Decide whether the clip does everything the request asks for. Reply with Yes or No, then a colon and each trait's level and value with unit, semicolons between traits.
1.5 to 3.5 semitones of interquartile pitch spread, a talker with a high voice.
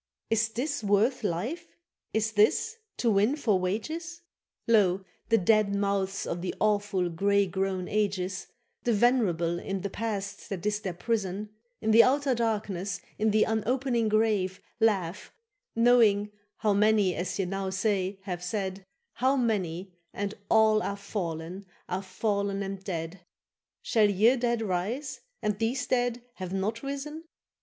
Yes: average, 3.1 semitones; high, 205 Hz